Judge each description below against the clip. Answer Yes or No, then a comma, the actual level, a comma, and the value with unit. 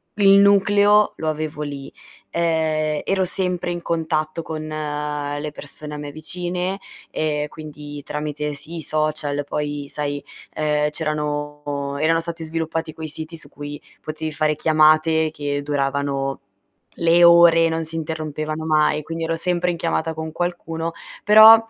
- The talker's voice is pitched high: No, medium, 155 Hz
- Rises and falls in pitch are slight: Yes, narrow, 1.9 semitones